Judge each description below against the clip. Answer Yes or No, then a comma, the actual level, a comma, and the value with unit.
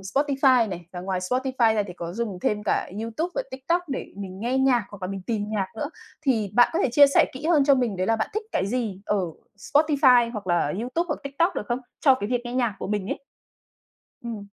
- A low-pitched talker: No, high, 235 Hz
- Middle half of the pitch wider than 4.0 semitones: Yes, average, 5.1 semitones